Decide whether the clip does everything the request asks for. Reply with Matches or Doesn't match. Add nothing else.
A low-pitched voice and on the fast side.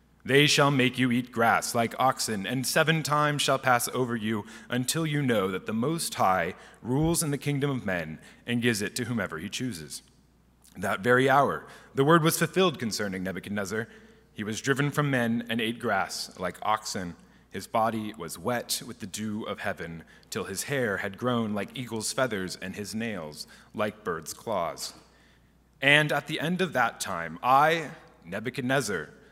Doesn't match